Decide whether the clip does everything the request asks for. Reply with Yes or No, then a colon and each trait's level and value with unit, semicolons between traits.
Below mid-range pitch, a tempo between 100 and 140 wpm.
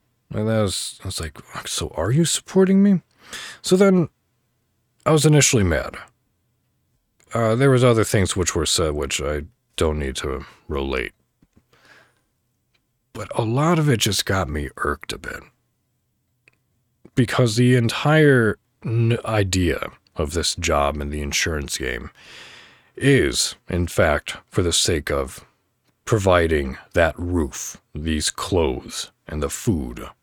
Yes: low, 115 Hz; slow, 135 wpm